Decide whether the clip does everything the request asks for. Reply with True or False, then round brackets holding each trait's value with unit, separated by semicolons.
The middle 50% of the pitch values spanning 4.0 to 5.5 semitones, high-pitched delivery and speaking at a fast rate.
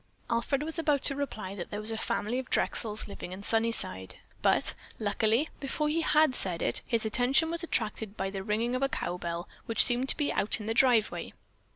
True (4.9 semitones; 230 Hz; 210 wpm)